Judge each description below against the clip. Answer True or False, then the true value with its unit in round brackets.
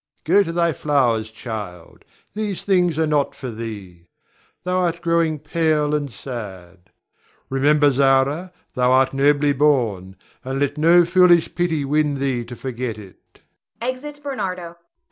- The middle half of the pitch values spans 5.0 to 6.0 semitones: True (5.3 semitones)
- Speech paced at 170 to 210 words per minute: False (140 wpm)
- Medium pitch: True (145 Hz)